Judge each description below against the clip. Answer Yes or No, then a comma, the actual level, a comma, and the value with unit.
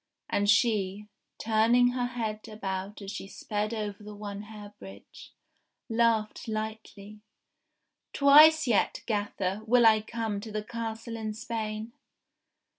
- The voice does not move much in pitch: Yes, narrow, 1.8 semitones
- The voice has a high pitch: Yes, high, 215 Hz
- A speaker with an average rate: No, slow, 130 wpm